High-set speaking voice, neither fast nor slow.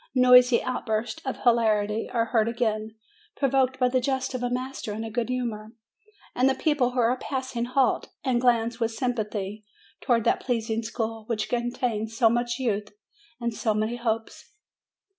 Yes: high, 235 Hz; average, 165 wpm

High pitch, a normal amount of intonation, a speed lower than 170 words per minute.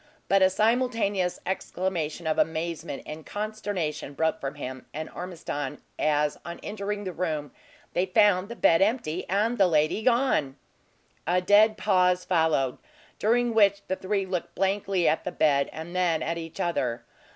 No: medium, 180 Hz; average, 4.4 semitones; average, 155 wpm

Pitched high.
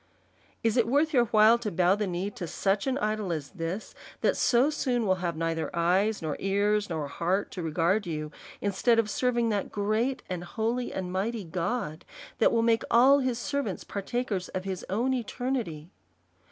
Yes: high, 205 Hz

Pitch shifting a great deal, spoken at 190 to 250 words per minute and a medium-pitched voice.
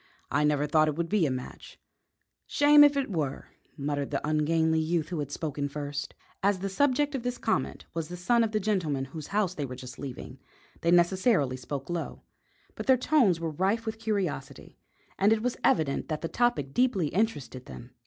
Yes: wide, 6.8 semitones; average, 195 wpm; medium, 165 Hz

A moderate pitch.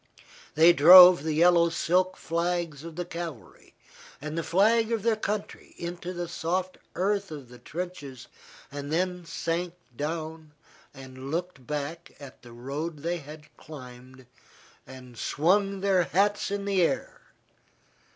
Yes: medium, 170 Hz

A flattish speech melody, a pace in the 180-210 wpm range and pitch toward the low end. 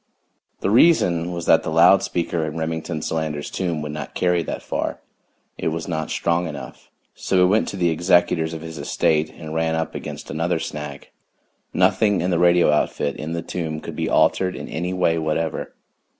Yes: narrow, 2.0 semitones; average, 190 wpm; very low, 80 Hz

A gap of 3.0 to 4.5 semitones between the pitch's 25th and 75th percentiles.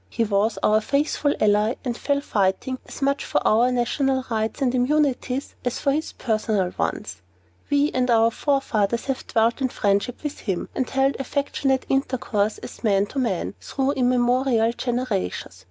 Yes: average, 3.8 semitones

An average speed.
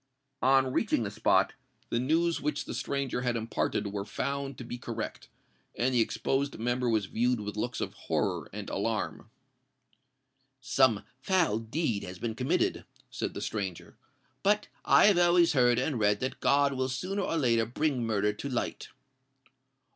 Yes: average, 160 wpm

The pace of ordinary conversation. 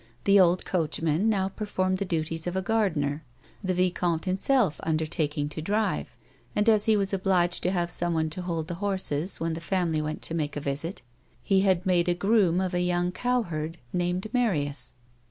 Yes: average, 185 wpm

